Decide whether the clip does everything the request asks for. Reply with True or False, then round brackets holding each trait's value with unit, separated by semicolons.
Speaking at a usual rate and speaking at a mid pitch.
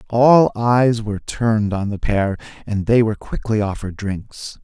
False (170 wpm; 110 Hz)